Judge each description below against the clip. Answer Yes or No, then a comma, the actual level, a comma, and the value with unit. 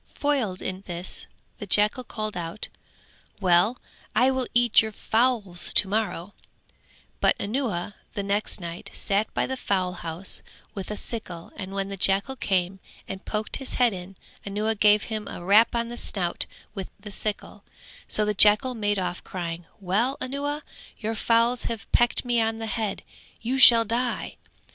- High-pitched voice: Yes, high, 210 Hz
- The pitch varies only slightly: No, average, 3.5 semitones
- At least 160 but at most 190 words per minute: Yes, average, 165 wpm